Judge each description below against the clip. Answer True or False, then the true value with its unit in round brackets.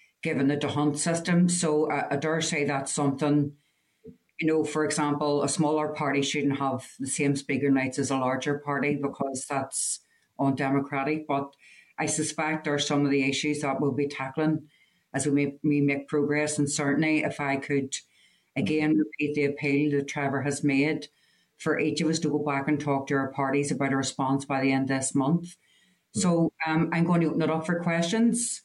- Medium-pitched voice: True (145 Hz)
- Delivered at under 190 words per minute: False (195 wpm)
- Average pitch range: False (1.8 semitones)